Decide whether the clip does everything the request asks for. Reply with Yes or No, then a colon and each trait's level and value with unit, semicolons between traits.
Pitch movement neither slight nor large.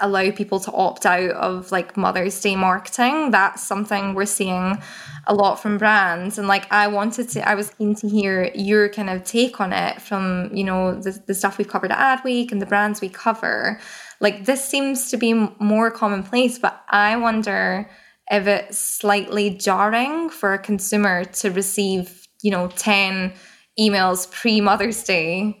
No: narrow, 1.8 semitones